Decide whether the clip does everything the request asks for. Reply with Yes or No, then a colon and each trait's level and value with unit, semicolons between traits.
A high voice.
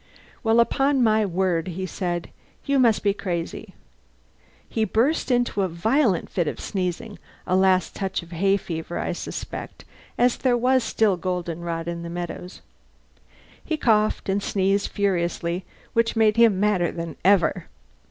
Yes: high, 195 Hz